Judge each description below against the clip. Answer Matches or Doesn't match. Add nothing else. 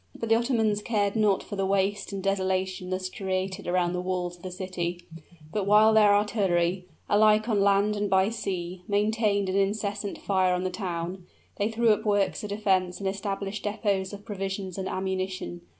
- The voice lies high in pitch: Matches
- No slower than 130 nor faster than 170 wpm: Doesn't match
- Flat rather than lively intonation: Matches